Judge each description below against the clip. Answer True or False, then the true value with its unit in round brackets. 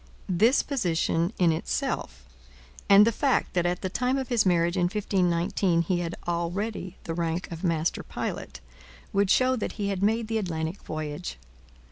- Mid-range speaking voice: True (180 Hz)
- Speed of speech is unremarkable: True (165 wpm)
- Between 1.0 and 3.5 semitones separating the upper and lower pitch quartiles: False (3.9 semitones)